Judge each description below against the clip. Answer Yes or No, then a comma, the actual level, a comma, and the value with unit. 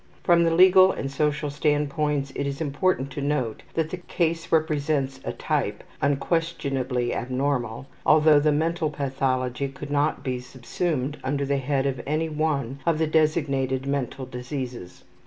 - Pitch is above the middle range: No, medium, 145 Hz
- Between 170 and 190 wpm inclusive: No, average, 150 wpm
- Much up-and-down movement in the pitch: No, average, 2.7 semitones